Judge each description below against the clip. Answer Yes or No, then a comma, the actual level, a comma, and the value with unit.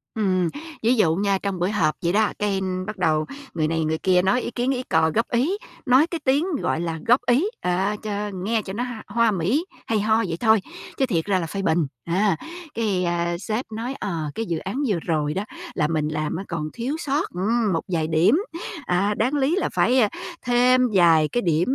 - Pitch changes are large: Yes, wide, 6.0 semitones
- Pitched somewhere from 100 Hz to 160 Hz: No, high, 200 Hz